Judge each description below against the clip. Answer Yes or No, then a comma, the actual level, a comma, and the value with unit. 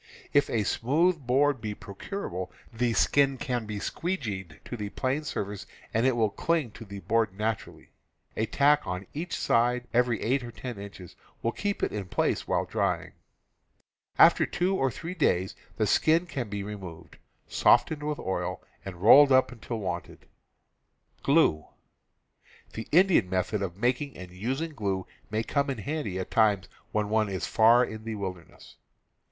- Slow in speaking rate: No, average, 170 wpm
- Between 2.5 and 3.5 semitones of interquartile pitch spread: No, wide, 5.6 semitones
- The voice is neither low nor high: No, low, 115 Hz